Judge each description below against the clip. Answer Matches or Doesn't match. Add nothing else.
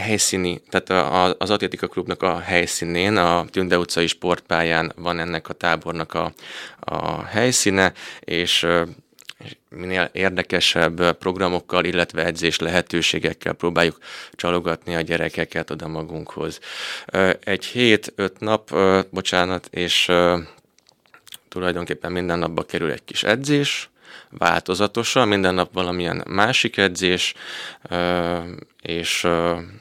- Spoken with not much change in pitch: Matches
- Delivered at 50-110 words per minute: Matches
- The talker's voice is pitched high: Doesn't match